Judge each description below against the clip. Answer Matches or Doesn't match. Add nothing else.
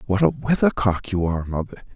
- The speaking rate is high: Doesn't match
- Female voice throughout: Doesn't match